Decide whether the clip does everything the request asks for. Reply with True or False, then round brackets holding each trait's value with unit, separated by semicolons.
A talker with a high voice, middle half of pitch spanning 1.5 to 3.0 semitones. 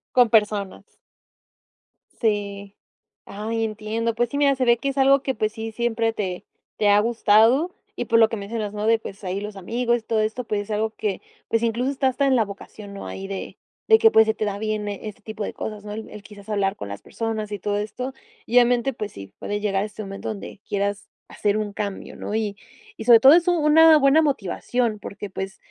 True (215 Hz; 2.7 semitones)